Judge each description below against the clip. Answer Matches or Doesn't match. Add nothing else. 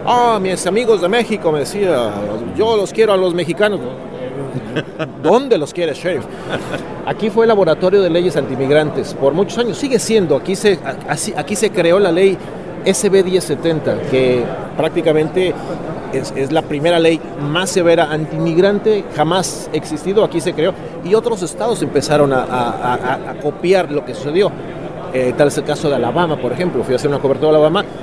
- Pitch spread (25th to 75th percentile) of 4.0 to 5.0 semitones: Matches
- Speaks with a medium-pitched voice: Matches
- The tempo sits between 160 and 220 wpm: Matches